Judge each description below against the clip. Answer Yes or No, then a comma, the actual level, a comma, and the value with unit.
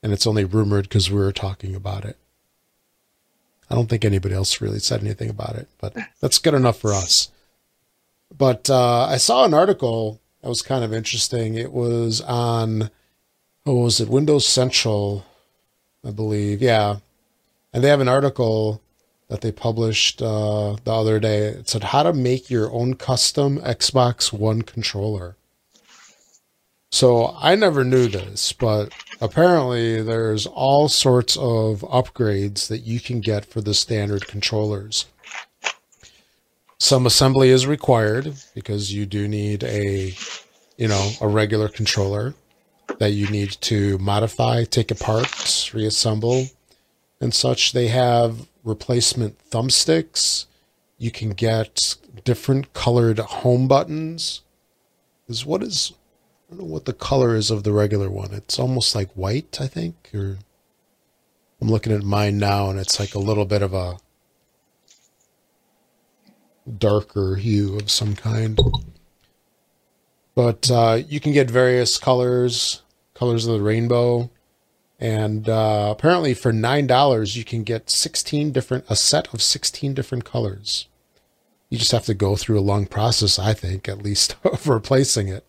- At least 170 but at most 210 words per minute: No, average, 145 wpm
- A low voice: Yes, low, 110 Hz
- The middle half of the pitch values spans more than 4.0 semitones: No, average, 3.1 semitones